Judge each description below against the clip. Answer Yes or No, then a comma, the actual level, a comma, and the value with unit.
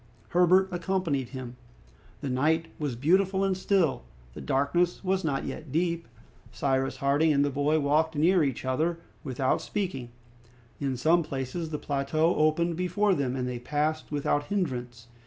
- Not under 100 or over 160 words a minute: Yes, average, 155 wpm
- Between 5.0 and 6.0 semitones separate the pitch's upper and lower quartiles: No, average, 4.3 semitones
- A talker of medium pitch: Yes, medium, 155 Hz